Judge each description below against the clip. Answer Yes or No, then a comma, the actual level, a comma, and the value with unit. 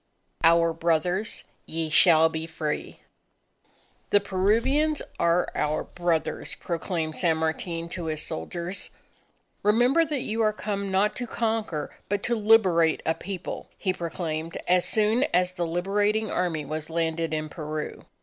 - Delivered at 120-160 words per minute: Yes, average, 140 wpm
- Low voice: No, medium, 175 Hz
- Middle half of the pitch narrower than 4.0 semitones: No, average, 4.3 semitones